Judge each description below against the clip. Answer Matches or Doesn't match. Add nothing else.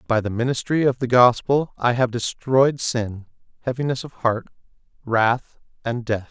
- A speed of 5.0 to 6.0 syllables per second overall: Doesn't match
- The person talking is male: Matches